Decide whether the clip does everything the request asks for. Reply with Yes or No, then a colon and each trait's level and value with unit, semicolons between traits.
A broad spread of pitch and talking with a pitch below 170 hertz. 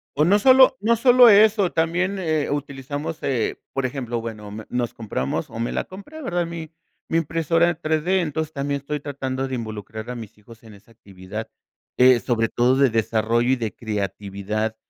Yes: wide, 6.7 semitones; low, 135 Hz